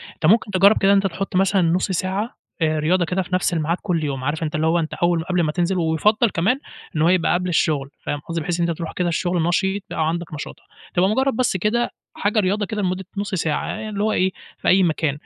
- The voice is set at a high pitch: No, medium, 180 Hz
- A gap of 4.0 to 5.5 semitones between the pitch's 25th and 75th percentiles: No, average, 3.3 semitones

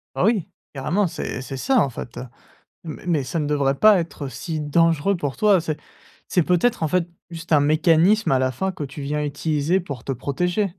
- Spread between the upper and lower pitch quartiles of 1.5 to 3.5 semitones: No, average, 4.0 semitones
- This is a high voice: No, medium, 160 Hz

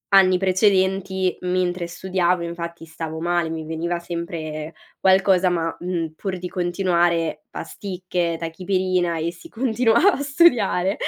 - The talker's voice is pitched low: No, medium, 180 Hz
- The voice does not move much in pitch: Yes, narrow, 2.0 semitones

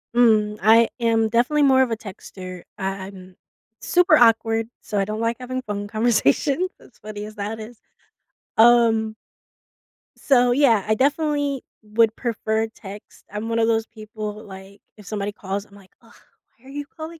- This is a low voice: No, high, 225 Hz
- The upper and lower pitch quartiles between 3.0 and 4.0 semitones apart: No, narrow, 2.6 semitones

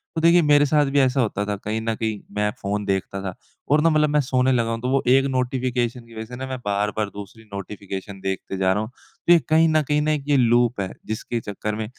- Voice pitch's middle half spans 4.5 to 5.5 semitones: Yes, average, 4.9 semitones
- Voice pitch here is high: No, low, 120 Hz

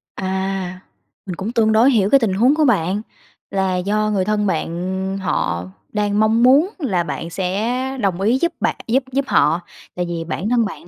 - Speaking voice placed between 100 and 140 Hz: No, high, 200 Hz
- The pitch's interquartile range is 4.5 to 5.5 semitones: No, average, 4.0 semitones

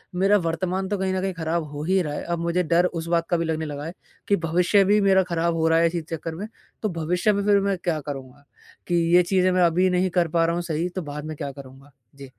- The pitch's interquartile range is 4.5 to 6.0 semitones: No, narrow, 2.6 semitones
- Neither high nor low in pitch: Yes, medium, 170 Hz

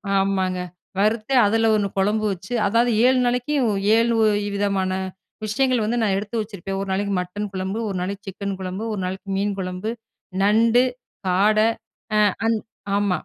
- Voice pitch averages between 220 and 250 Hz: No, high, 205 Hz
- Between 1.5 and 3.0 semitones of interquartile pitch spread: Yes, average, 2.7 semitones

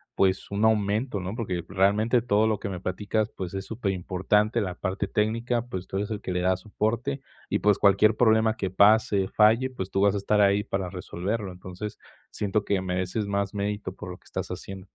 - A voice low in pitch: Yes, low, 100 Hz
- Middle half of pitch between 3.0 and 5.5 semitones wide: No, narrow, 2.5 semitones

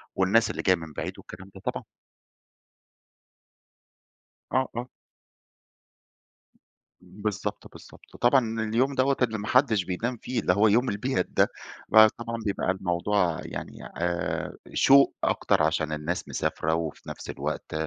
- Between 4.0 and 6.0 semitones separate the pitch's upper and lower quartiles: Yes, average, 4.9 semitones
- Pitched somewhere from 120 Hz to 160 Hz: No, low, 105 Hz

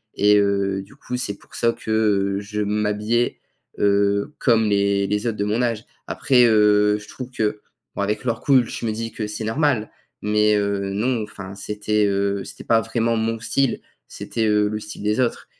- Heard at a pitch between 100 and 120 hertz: Yes, low, 105 Hz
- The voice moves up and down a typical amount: No, narrow, 1.9 semitones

